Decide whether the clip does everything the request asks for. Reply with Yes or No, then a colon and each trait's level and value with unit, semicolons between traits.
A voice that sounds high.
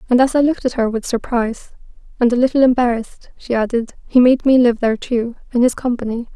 Yes: high, 240 Hz